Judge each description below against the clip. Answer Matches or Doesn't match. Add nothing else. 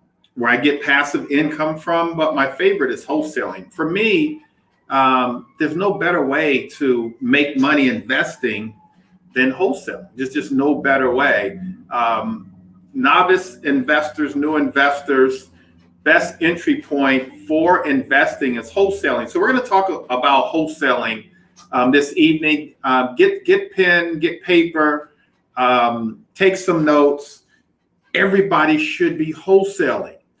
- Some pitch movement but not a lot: Doesn't match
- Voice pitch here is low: Doesn't match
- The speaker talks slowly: Matches